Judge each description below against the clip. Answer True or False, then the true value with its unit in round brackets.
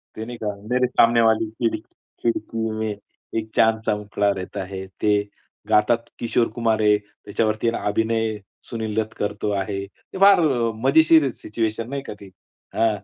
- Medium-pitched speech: False (110 Hz)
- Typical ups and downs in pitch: False (1.9 semitones)